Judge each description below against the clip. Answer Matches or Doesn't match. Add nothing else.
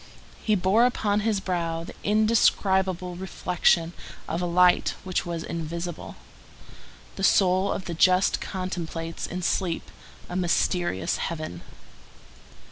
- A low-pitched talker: Doesn't match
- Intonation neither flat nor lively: Doesn't match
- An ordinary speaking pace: Doesn't match